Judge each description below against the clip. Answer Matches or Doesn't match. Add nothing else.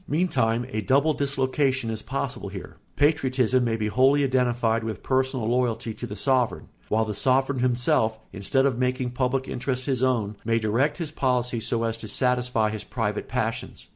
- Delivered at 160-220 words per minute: Matches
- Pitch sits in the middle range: Doesn't match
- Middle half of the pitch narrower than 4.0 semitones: Matches